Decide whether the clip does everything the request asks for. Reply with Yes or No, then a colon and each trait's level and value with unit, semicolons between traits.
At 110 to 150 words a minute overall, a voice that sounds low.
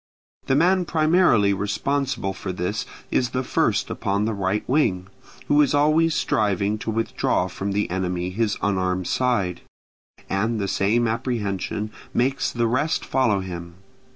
Yes: average, 145 wpm; low, 105 Hz